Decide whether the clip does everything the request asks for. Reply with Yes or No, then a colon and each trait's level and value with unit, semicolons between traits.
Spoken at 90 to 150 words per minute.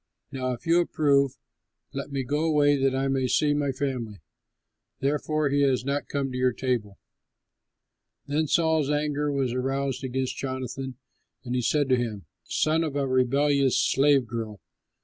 No: average, 160 wpm